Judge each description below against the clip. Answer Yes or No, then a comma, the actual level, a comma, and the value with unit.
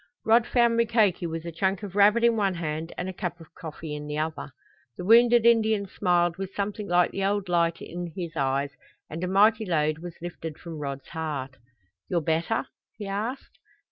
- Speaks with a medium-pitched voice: Yes, medium, 175 Hz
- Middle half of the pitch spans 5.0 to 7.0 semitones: No, average, 4.3 semitones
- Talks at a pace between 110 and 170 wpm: No, average, 195 wpm